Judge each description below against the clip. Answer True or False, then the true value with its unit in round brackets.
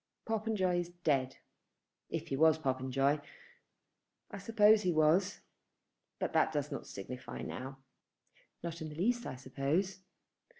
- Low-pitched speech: False (160 Hz)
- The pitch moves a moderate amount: False (5.8 semitones)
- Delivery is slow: True (130 wpm)